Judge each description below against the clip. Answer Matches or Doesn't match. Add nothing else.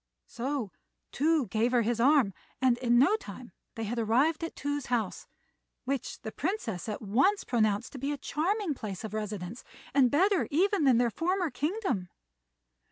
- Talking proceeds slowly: Doesn't match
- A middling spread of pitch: Doesn't match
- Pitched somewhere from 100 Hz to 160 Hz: Doesn't match